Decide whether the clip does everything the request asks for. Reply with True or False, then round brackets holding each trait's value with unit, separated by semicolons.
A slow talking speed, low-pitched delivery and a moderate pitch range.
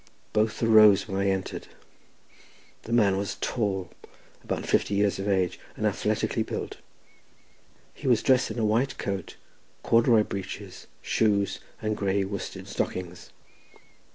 False (130 wpm; 100 Hz; 2.2 semitones)